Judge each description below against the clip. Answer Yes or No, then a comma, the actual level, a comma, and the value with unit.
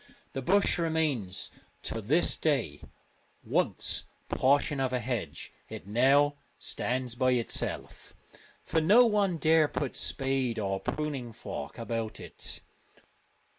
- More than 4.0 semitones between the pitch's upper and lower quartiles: Yes, average, 4.8 semitones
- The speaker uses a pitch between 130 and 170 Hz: Yes, low, 135 Hz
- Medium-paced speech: No, slow, 120 wpm